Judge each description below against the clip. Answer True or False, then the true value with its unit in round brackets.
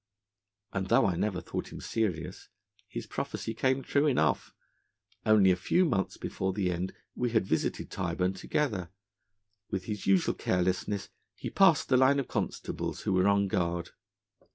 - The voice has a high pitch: False (100 Hz)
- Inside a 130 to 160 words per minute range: True (155 wpm)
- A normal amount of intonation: True (4.4 semitones)